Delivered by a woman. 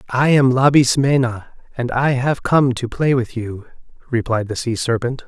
No: male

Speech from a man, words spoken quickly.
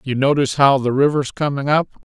No: male; average, 195 wpm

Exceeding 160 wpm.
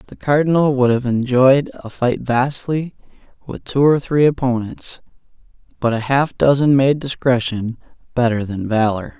No: average, 145 wpm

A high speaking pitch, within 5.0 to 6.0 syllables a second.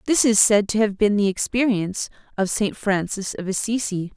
Yes: high, 205 Hz; 5.2 syllables/s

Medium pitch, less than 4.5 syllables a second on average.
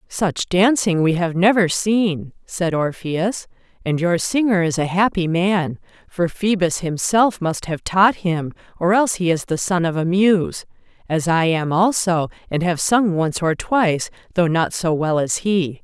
Yes: medium, 175 Hz; 4.1 syllables/s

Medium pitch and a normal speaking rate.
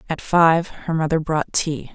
Yes: medium, 160 Hz; average, 185 wpm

